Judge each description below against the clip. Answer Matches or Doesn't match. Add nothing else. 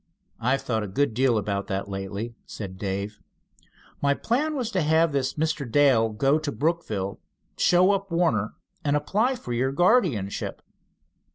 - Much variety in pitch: Matches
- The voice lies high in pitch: Doesn't match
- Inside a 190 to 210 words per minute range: Doesn't match